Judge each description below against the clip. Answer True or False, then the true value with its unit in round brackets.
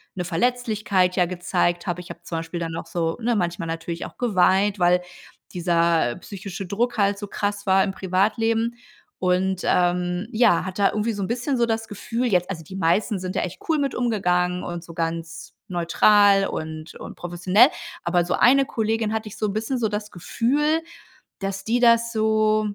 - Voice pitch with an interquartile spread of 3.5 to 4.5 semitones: True (3.9 semitones)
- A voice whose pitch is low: False (195 Hz)